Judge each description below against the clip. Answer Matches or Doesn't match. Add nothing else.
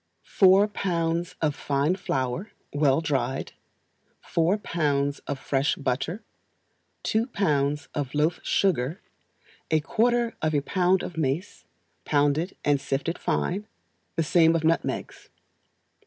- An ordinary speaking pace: Doesn't match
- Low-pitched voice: Doesn't match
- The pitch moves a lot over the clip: Doesn't match